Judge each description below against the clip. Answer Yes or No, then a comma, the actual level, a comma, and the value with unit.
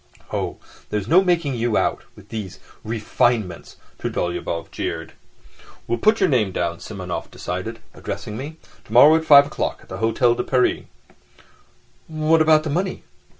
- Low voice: Yes, low, 120 Hz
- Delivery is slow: No, average, 150 wpm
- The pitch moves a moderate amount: No, wide, 6.8 semitones